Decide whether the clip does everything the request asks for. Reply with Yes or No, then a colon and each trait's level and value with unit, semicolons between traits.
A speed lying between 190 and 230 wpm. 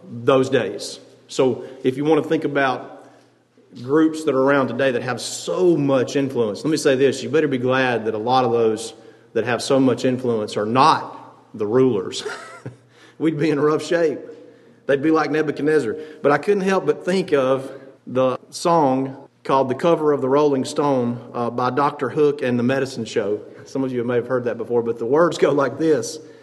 Yes: average, 200 wpm